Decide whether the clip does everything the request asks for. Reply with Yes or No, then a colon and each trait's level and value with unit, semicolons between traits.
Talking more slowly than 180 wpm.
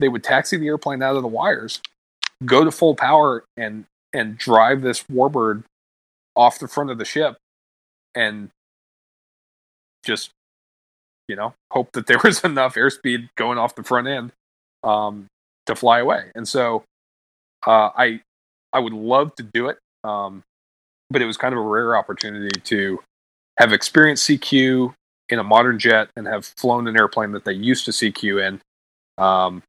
Yes: average, 165 wpm